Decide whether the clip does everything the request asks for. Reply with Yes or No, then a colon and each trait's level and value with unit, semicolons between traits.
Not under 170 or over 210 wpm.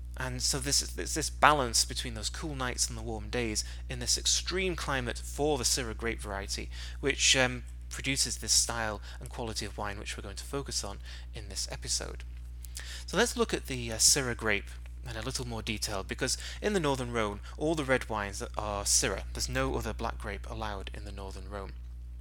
Yes: fast, 205 wpm